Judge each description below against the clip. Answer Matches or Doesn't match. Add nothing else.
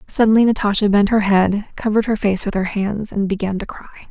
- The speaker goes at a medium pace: Doesn't match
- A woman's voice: Matches